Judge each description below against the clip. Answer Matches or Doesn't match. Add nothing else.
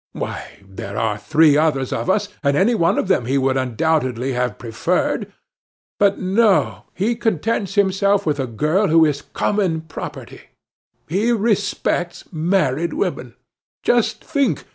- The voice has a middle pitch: Matches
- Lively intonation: Matches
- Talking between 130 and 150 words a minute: Matches